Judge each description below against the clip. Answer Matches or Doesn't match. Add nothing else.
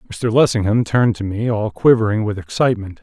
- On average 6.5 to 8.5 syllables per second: Doesn't match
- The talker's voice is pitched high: Doesn't match